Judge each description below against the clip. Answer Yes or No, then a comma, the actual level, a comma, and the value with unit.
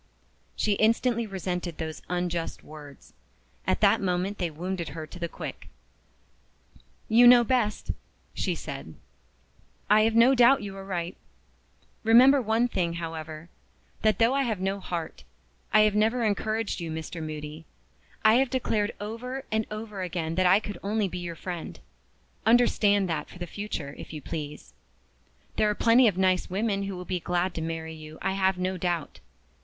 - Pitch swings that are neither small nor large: Yes, average, 4.5 semitones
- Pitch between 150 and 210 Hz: Yes, high, 190 Hz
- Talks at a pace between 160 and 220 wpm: Yes, average, 170 wpm